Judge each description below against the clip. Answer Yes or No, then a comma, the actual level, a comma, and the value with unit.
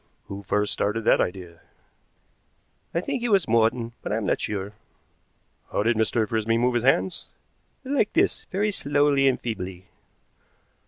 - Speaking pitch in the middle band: No, low, 115 Hz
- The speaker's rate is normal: Yes, average, 155 wpm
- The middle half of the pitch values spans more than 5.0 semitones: Yes, wide, 5.6 semitones